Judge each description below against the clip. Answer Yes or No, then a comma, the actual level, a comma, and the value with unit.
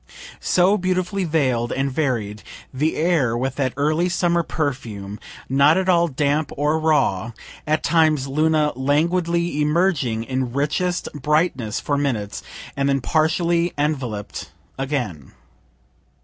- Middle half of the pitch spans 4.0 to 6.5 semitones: Yes, average, 4.5 semitones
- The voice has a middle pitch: Yes, medium, 150 Hz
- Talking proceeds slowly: Yes, slow, 120 wpm